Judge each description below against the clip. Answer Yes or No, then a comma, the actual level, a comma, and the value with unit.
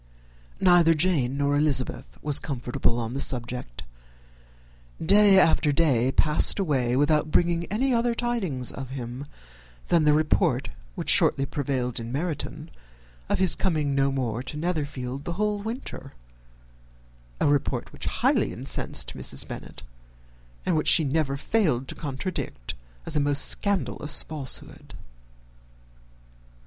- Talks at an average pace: No, slow, 130 wpm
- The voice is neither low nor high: Yes, medium, 145 Hz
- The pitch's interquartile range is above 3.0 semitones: Yes, average, 4.5 semitones